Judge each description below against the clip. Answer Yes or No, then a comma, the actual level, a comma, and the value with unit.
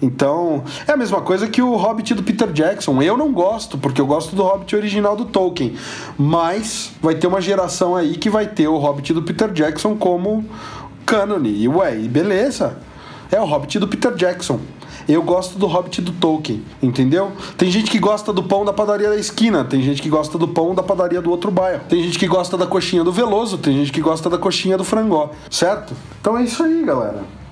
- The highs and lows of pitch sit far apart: No, average, 4.3 semitones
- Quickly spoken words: Yes, fast, 210 wpm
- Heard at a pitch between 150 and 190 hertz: Yes, medium, 185 Hz